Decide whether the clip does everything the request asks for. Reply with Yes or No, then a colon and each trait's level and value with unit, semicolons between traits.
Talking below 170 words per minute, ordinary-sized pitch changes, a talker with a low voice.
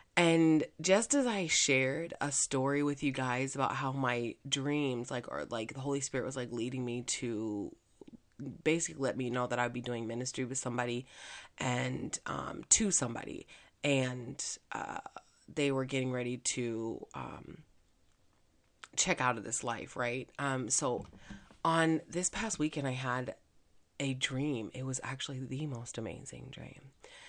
Yes: average, 155 wpm; average, 3.0 semitones; low, 130 Hz